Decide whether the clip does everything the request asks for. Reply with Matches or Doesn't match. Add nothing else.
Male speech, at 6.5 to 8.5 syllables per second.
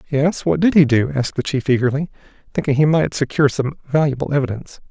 Matches